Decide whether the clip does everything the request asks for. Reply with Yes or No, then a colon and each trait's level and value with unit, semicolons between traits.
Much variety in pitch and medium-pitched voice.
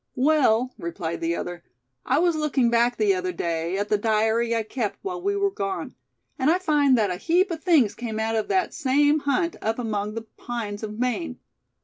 No: wide, 6.4 semitones; high, 235 Hz